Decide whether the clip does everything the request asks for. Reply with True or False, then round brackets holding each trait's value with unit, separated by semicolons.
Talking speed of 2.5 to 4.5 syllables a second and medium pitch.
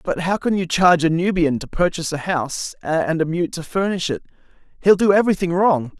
False (6.0 syllables/s; 170 Hz)